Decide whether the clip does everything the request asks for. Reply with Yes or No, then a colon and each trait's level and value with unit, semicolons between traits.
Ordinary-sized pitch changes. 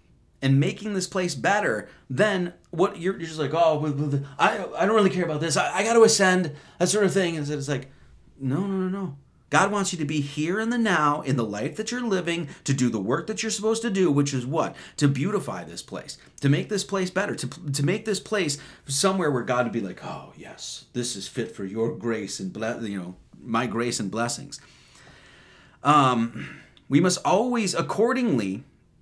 No: wide, 6.6 semitones